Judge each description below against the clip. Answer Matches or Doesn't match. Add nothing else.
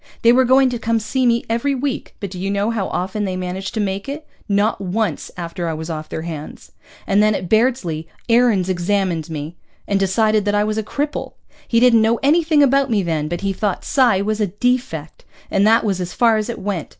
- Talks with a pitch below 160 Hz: Doesn't match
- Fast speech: Matches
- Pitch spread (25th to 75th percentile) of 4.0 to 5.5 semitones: Matches